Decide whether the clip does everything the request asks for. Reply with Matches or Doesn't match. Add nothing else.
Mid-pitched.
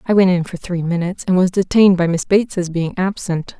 Matches